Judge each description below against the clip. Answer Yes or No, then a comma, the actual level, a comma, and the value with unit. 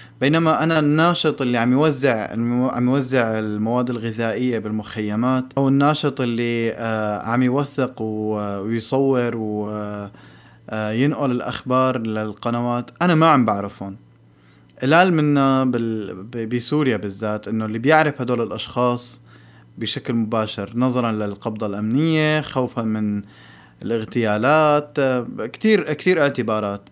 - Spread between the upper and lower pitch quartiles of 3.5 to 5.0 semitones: Yes, average, 3.9 semitones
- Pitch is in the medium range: No, low, 120 Hz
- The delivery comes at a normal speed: Yes, average, 110 wpm